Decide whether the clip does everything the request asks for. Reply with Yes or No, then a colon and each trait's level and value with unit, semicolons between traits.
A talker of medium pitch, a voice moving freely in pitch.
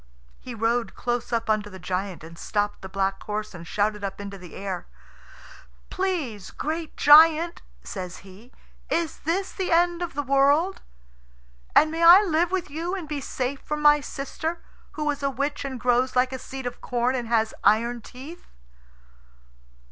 No: very high, 260 Hz; wide, 6.9 semitones